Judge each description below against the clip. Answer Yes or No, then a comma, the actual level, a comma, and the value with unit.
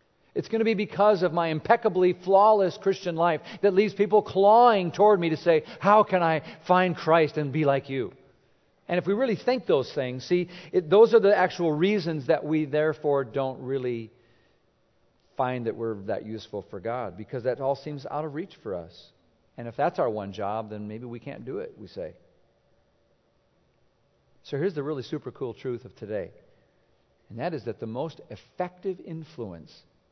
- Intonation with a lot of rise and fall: Yes, wide, 7.1 semitones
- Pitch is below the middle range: No, medium, 160 Hz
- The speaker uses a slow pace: No, average, 185 wpm